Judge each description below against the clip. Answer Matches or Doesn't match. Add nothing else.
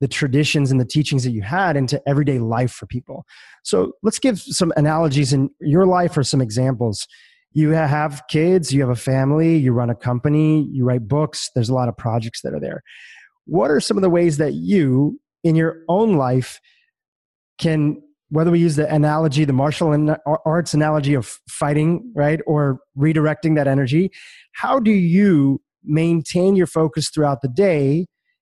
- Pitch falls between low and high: Matches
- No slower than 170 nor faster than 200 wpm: Matches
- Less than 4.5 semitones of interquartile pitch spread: Matches